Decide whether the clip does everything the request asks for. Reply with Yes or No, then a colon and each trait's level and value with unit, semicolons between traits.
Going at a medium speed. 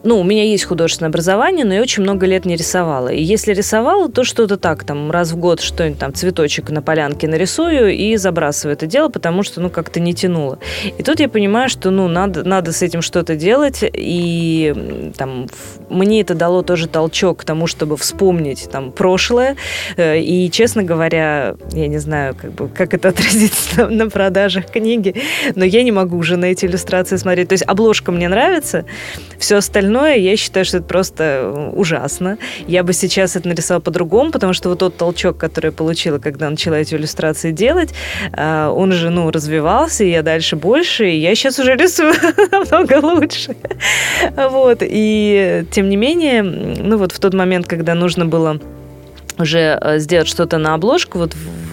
No: fast, 180 wpm